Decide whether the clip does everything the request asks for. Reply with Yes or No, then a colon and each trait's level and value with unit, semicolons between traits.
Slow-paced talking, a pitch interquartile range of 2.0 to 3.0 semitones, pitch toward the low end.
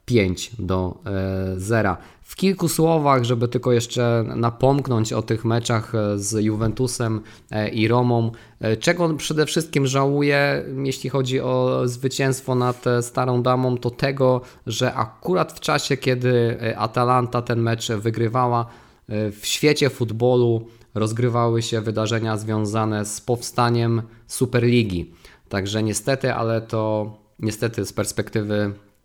No: average, 120 wpm; narrow, 2.6 semitones; low, 120 Hz